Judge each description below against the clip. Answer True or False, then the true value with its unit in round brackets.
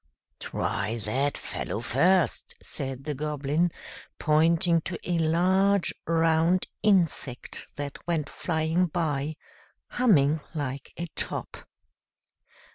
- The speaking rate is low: True (100 wpm)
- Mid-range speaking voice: True (160 Hz)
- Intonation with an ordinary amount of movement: True (3.4 semitones)